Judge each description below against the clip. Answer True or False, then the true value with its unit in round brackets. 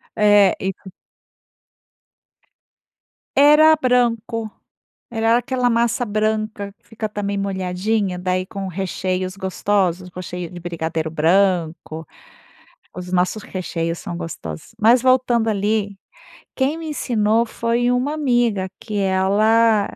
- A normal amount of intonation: True (4.0 semitones)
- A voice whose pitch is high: True (205 Hz)